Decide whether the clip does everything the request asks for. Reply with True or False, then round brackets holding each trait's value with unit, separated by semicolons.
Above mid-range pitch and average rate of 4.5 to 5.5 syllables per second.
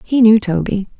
True (210 Hz; 4.9 syllables/s)